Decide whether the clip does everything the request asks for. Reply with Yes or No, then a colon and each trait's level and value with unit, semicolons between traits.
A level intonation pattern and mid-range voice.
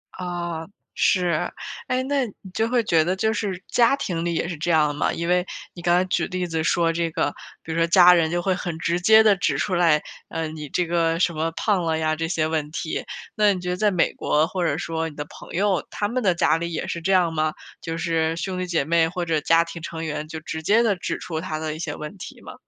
Yes: narrow, 2.2 semitones; medium, 170 Hz